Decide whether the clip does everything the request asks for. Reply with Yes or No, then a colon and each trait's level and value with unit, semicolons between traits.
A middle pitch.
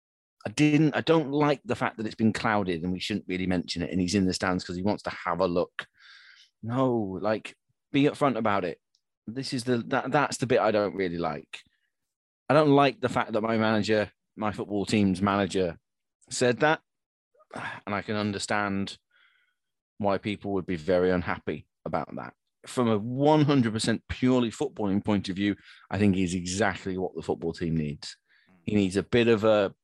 No: low, 105 Hz